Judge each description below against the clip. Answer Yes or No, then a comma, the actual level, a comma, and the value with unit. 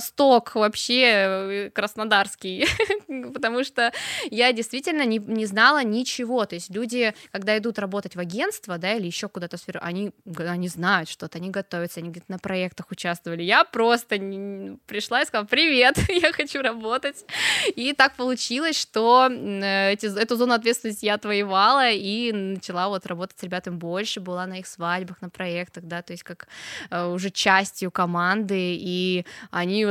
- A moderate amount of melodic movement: Yes, average, 4.5 semitones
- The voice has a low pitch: No, high, 200 Hz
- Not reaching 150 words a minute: Yes, average, 135 wpm